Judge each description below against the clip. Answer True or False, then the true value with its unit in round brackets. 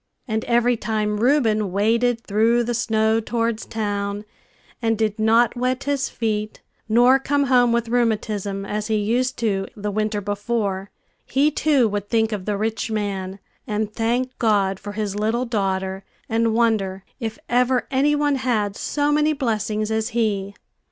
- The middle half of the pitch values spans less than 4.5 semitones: True (2.7 semitones)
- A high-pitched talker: True (220 Hz)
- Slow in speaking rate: False (160 wpm)